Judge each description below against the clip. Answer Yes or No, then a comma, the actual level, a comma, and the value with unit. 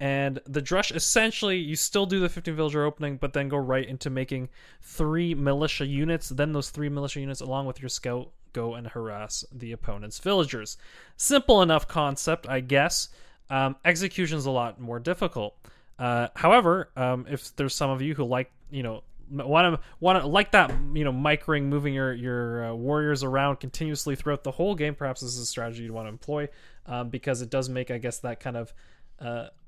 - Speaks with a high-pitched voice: No, medium, 140 Hz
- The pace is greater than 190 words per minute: Yes, average, 200 wpm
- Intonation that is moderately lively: Yes, average, 3.6 semitones